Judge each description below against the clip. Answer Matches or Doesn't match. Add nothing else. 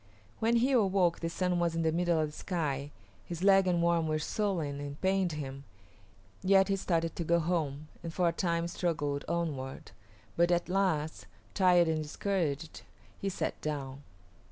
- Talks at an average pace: Matches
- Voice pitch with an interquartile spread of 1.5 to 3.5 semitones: Matches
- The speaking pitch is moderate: Matches